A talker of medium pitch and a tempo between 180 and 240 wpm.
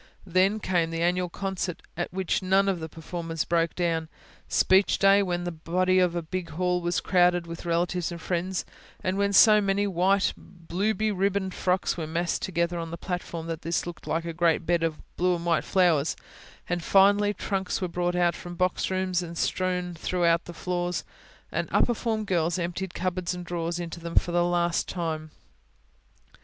Yes: medium, 175 Hz; average, 185 wpm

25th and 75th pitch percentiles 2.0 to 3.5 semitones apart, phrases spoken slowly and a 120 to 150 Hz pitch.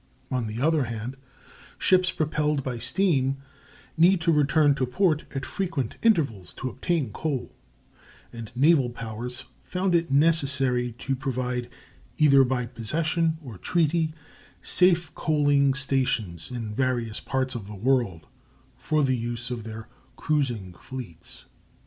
No: average, 4.5 semitones; slow, 130 wpm; low, 135 Hz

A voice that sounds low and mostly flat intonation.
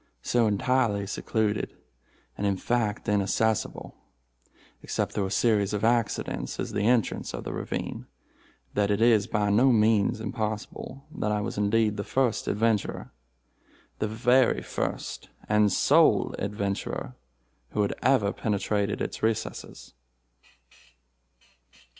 Yes: low, 105 Hz; narrow, 1.9 semitones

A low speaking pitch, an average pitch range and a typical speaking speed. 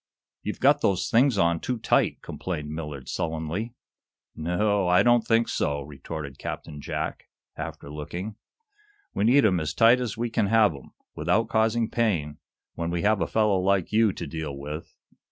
No: very low, 95 Hz; wide, 6.3 semitones; average, 175 wpm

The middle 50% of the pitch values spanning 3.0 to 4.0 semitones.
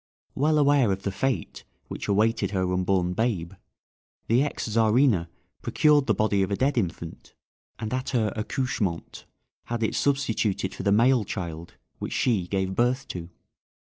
No: average, 5.2 semitones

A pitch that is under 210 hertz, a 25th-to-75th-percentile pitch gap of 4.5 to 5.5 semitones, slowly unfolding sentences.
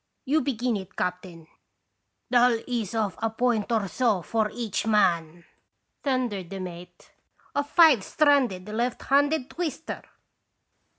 No: high, 225 Hz; average, 5.2 semitones; slow, 125 wpm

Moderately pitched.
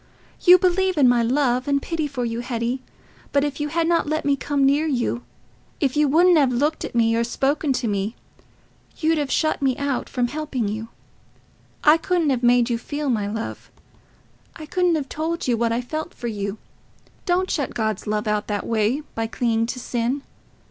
No: very high, 265 Hz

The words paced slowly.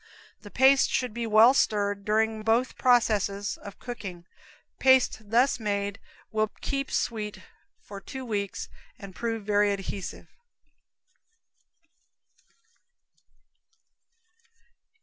Yes: slow, 95 wpm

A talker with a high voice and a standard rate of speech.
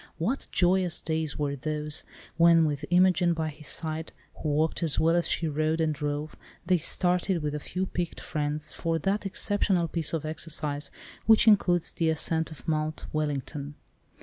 No: medium, 160 Hz; average, 170 wpm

